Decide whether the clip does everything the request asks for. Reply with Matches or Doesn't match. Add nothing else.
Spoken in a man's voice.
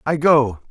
Matches